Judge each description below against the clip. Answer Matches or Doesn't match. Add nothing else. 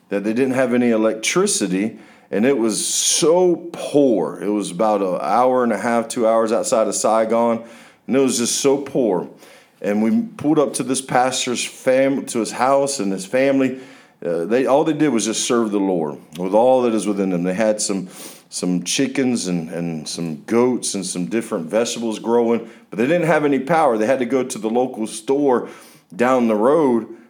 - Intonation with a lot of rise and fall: Doesn't match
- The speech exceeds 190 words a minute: Matches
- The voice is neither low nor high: Doesn't match